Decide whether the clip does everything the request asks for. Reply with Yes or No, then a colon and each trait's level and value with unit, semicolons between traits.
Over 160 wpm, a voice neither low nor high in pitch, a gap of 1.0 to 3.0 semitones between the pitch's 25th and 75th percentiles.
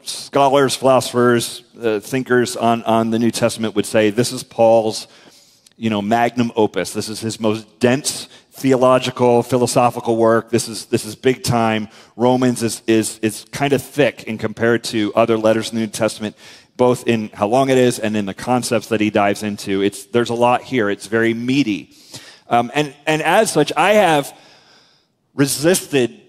No: average, 180 wpm; low, 115 Hz; narrow, 2.4 semitones